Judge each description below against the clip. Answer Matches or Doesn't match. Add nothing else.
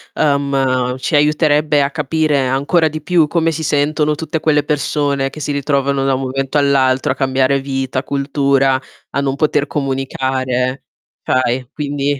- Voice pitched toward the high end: Doesn't match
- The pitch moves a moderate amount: Doesn't match